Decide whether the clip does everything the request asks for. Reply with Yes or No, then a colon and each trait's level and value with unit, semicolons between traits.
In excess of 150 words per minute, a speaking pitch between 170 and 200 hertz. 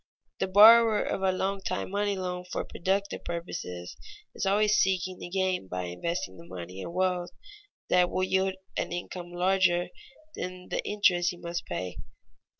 Yes: average, 165 wpm; medium, 185 Hz